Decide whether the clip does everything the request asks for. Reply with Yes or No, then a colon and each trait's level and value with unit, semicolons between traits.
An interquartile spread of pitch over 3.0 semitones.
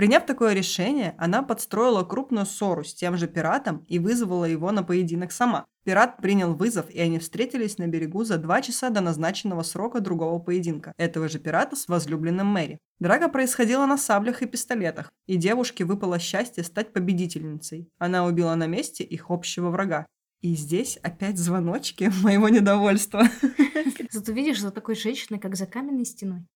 Yes: average, 4.9 semitones